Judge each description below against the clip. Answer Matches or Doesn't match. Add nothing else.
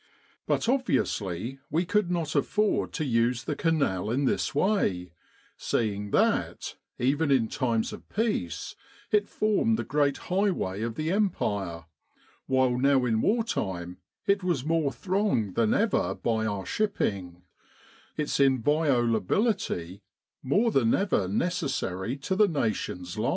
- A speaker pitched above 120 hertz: Matches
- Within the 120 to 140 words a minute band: Matches